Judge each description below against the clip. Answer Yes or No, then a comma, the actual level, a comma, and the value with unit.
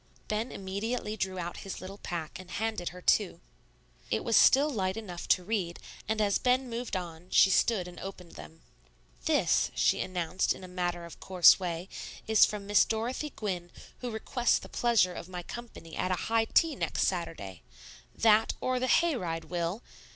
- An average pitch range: Yes, average, 4.2 semitones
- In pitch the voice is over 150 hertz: Yes, high, 190 Hz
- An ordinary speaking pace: Yes, average, 180 wpm